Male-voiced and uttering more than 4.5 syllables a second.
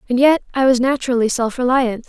No: female; 6.2 syllables/s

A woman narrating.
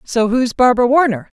Yes: female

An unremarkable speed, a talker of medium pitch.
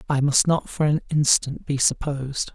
Yes: average, 190 wpm; medium, 145 Hz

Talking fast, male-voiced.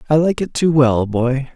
Yes: fast, 230 wpm; male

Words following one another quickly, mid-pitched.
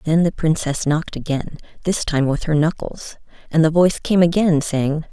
No: average, 190 wpm; medium, 160 Hz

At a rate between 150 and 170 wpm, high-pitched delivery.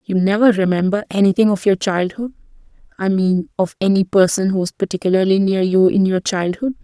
Yes: average, 165 wpm; high, 195 Hz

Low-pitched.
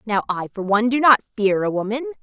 No: high, 225 Hz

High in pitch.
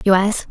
Yes: high, 195 Hz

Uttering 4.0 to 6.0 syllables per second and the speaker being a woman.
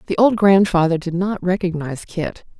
Yes: 5.4 syllables/s; female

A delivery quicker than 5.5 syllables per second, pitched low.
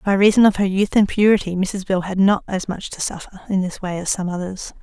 No: 5.7 syllables/s; high, 190 Hz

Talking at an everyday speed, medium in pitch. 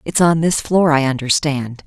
Yes: average, 195 wpm; medium, 150 Hz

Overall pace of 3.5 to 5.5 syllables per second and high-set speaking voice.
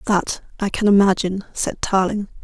Yes: 5.0 syllables/s; high, 195 Hz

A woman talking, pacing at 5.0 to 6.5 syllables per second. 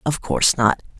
Yes: female; 5.3 syllables/s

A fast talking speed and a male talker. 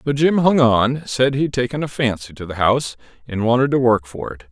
Yes: fast, 225 wpm; male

